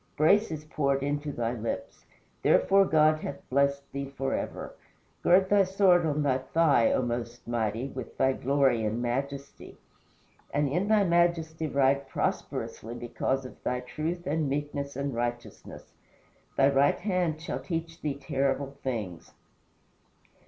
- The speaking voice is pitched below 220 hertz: Yes, medium, 140 Hz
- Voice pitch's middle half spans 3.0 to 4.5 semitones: Yes, average, 3.6 semitones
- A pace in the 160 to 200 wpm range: No, average, 140 wpm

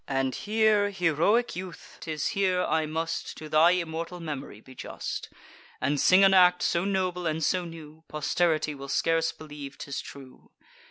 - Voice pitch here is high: No, medium, 165 Hz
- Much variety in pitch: No, average, 3.3 semitones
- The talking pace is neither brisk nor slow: Yes, average, 160 wpm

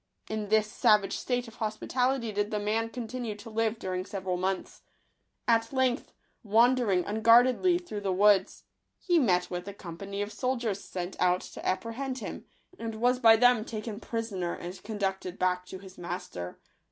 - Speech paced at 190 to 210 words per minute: No, average, 165 wpm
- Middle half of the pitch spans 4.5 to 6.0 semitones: No, average, 3.7 semitones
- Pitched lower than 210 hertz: No, high, 215 Hz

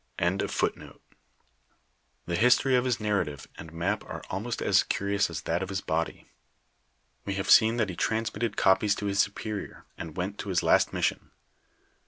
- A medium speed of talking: Yes, average, 165 wpm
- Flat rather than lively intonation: No, average, 3.6 semitones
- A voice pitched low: Yes, low, 100 Hz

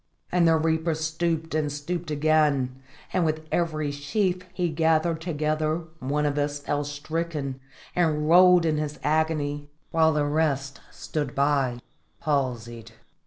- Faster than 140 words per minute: No, slow, 135 wpm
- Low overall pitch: No, medium, 155 Hz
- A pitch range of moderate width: No, narrow, 2.0 semitones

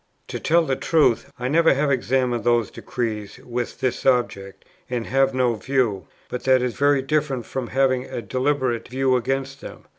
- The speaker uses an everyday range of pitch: No, narrow, 2.1 semitones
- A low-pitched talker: Yes, low, 130 Hz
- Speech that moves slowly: No, average, 175 wpm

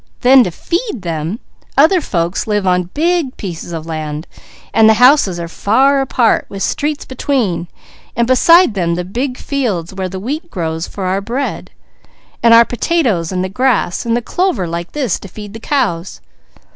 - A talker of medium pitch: No, high, 215 Hz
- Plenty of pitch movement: Yes, wide, 7.2 semitones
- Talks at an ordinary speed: Yes, average, 170 wpm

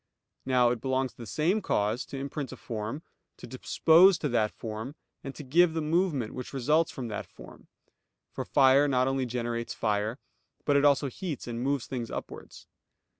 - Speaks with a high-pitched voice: No, low, 130 Hz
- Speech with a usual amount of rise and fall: Yes, average, 3.8 semitones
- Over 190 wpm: No, average, 180 wpm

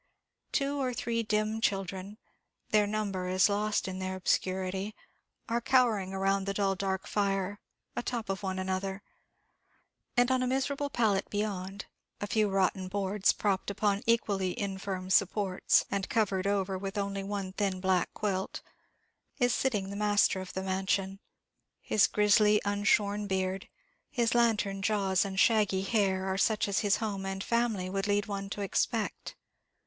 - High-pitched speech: Yes, high, 200 Hz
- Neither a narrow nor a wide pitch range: No, narrow, 1.9 semitones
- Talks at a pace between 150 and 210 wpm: Yes, average, 155 wpm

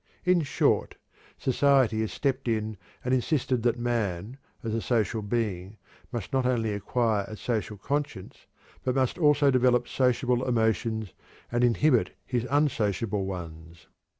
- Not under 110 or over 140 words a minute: Yes, slow, 135 wpm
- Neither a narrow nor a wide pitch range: Yes, average, 3.1 semitones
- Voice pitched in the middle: No, low, 120 Hz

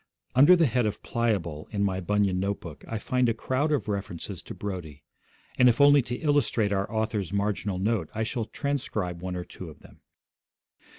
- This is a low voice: Yes, low, 105 Hz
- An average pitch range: Yes, average, 4.7 semitones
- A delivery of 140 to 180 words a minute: No, average, 190 wpm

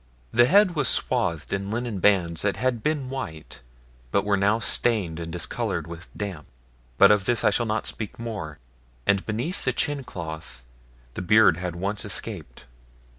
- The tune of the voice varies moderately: No, wide, 5.7 semitones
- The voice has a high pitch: No, low, 100 Hz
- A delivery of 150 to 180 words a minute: Yes, average, 170 wpm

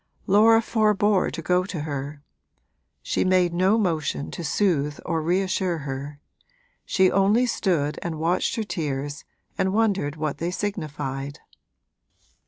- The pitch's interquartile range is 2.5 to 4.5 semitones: No, average, 4.9 semitones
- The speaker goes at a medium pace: No, slow, 130 wpm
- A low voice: No, medium, 175 Hz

